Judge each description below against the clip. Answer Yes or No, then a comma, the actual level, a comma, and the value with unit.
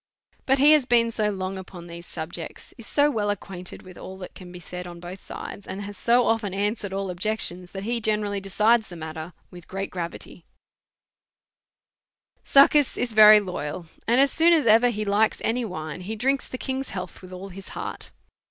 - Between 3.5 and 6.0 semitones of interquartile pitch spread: Yes, average, 4.2 semitones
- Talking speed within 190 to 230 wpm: Yes, average, 195 wpm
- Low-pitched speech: No, high, 200 Hz